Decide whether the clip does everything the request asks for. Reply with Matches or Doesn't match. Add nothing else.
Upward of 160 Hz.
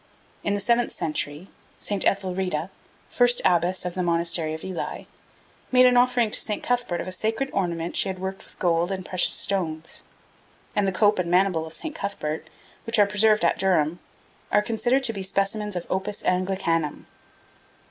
Matches